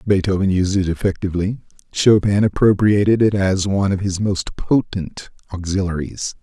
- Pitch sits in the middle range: No, very low, 95 Hz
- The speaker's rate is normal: No, slow, 130 wpm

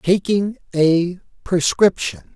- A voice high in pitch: No, medium, 175 Hz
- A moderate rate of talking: No, slow, 75 wpm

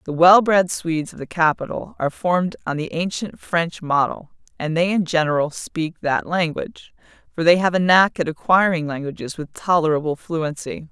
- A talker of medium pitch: Yes, medium, 165 Hz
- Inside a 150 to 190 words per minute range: Yes, average, 175 wpm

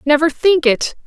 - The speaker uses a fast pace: No, average, 170 wpm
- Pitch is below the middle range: No, very high, 305 Hz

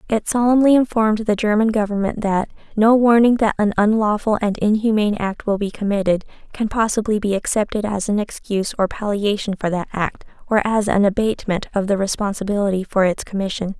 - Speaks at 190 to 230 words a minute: No, average, 175 wpm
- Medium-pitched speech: No, high, 210 Hz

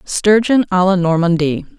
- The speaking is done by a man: No, female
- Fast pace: No, average, 170 wpm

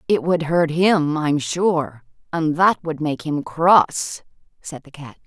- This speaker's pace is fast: No, average, 170 wpm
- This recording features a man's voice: No, female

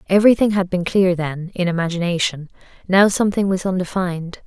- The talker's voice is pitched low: No, medium, 185 Hz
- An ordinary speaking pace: Yes, average, 150 wpm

